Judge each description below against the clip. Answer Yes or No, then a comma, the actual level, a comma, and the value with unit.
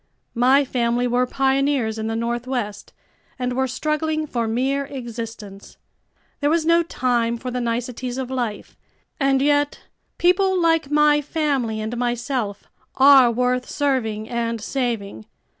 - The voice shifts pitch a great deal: No, average, 3.2 semitones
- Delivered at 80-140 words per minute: Yes, slow, 135 wpm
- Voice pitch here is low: No, very high, 250 Hz